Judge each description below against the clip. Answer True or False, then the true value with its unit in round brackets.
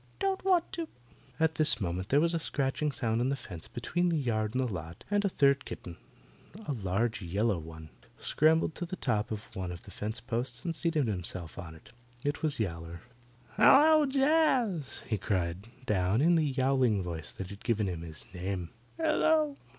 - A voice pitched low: True (120 Hz)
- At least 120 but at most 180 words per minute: False (190 wpm)